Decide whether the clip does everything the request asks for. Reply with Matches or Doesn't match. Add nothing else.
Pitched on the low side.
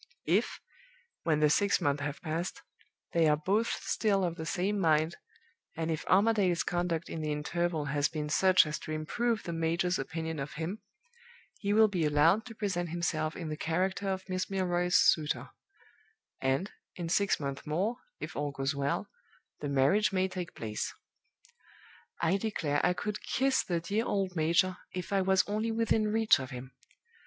Doesn't match